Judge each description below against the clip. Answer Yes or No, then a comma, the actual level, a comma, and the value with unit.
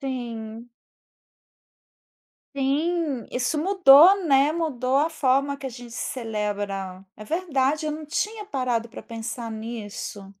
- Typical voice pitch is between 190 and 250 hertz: No, very high, 260 Hz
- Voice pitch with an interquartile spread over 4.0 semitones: Yes, average, 5.2 semitones